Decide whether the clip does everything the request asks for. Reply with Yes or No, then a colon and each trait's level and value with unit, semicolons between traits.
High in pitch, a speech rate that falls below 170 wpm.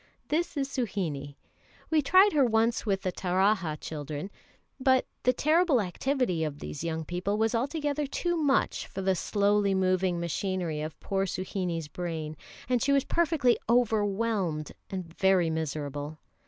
Yes: high, 195 Hz; average, 145 wpm